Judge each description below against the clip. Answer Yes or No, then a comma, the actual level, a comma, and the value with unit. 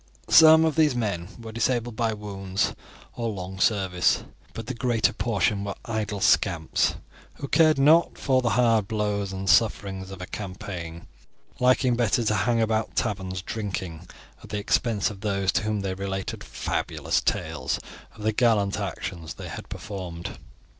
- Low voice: Yes, low, 105 Hz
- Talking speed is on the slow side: No, average, 160 wpm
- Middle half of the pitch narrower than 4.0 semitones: Yes, average, 3.4 semitones